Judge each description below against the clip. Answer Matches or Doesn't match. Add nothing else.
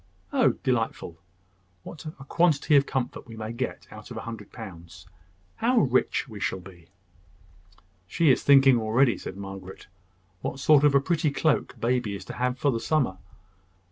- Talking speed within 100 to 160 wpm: Doesn't match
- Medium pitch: Doesn't match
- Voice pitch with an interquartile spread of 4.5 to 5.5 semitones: Matches